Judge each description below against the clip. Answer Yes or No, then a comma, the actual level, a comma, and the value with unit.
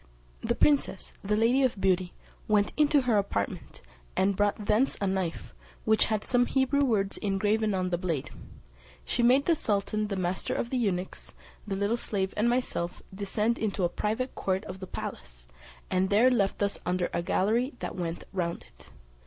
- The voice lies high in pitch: Yes, high, 205 Hz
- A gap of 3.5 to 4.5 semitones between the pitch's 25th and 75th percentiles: Yes, average, 4.0 semitones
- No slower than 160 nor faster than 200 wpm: Yes, average, 180 wpm